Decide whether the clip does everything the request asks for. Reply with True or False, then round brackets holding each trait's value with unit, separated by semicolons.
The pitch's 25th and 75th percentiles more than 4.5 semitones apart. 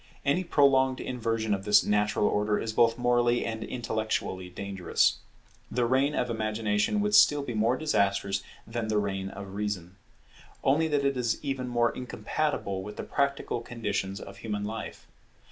False (3.8 semitones)